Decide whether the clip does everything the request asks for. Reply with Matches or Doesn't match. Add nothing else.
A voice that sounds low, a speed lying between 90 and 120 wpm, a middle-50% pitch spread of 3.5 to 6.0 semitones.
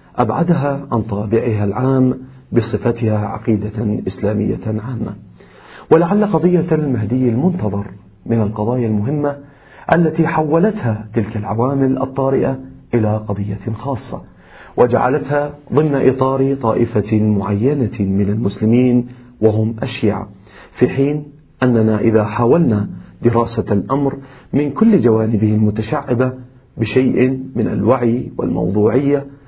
Matches